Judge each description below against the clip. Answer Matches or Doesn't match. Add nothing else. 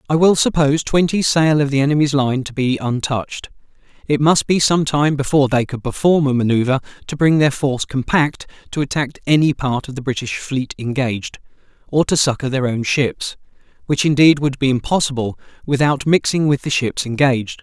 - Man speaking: Matches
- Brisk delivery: Doesn't match